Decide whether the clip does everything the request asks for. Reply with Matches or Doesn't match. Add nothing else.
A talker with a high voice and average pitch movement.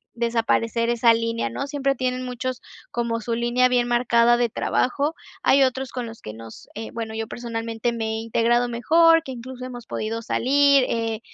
Doesn't match